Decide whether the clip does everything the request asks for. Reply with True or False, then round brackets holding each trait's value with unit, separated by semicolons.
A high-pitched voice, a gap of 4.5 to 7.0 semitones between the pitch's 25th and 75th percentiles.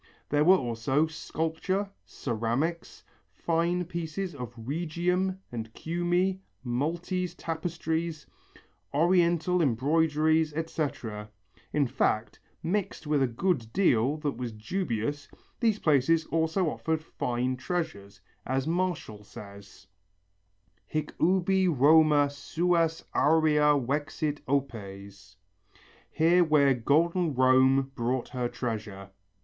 False (150 Hz; 5.3 semitones)